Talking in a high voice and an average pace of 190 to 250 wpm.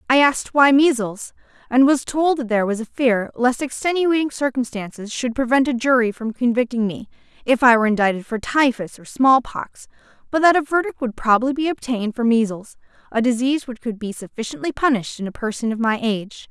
Yes: high, 245 Hz; average, 195 wpm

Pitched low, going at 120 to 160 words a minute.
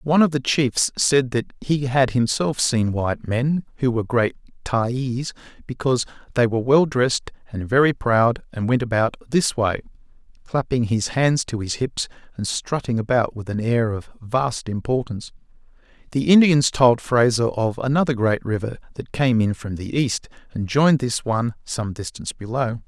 No: low, 120 Hz; average, 170 wpm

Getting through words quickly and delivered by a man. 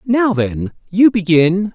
No: slow, 135 wpm; male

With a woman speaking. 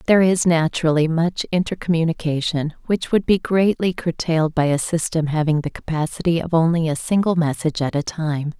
Yes: female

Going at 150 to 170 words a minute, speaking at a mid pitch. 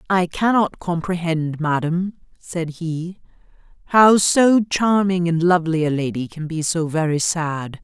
No: average, 140 wpm; medium, 170 Hz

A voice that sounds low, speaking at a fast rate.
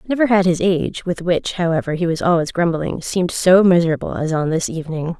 No: medium, 170 Hz; fast, 210 wpm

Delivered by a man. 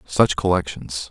Yes: male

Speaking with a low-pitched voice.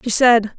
No: high, 230 Hz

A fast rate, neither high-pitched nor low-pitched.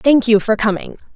No: fast, 210 wpm; high, 225 Hz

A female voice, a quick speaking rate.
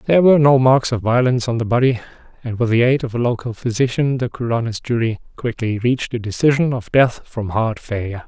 No: male; fast, 210 wpm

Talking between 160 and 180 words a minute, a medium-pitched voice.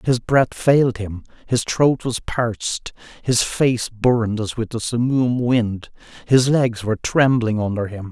No: average, 170 wpm; low, 115 Hz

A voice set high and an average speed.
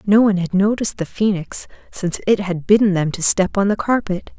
No: high, 195 Hz; fast, 220 wpm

